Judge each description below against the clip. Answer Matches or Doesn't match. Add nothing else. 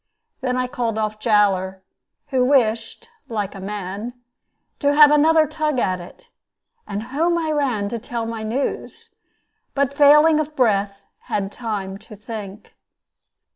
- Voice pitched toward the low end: Doesn't match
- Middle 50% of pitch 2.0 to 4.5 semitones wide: Doesn't match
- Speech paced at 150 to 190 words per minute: Doesn't match